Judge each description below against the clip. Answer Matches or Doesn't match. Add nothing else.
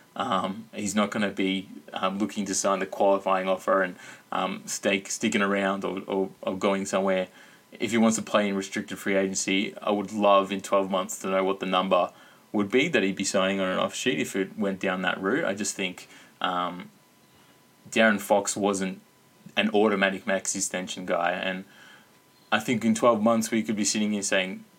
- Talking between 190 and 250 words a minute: Matches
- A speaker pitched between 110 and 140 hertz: Doesn't match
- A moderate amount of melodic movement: Doesn't match